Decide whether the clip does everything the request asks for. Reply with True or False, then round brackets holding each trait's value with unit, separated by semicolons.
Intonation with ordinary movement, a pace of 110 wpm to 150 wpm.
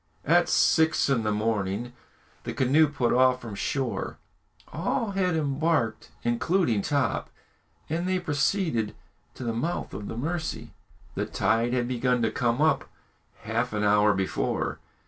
False (5.8 semitones; 145 wpm)